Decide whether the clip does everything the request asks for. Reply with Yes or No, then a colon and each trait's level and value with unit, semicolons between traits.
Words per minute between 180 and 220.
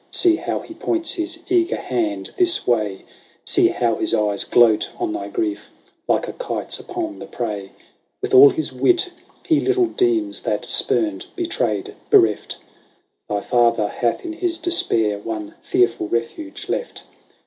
No: average, 150 wpm